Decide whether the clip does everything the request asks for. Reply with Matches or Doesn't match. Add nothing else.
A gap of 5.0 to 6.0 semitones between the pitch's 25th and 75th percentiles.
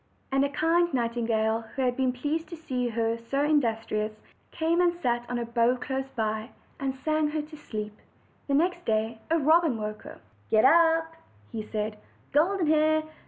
Matches